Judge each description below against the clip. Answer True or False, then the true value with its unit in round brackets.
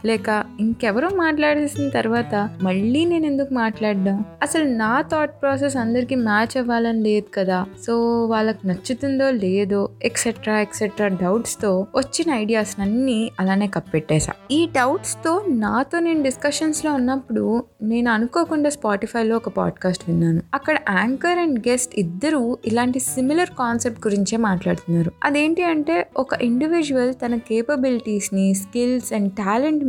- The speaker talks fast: True (130 wpm)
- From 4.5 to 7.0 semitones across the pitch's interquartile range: True (4.9 semitones)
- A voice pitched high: True (235 Hz)